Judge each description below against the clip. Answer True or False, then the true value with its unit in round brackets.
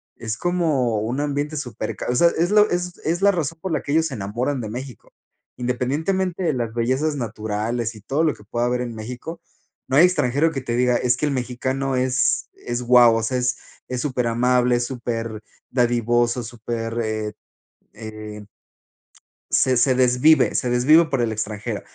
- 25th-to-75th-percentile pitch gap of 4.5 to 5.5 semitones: False (3.7 semitones)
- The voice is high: False (125 Hz)